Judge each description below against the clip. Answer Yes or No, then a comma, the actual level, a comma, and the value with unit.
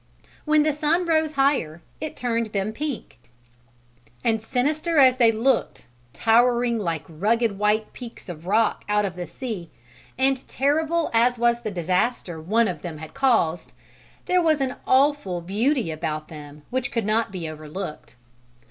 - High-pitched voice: Yes, high, 230 Hz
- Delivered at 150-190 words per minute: Yes, average, 155 wpm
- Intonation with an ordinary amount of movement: No, wide, 7.0 semitones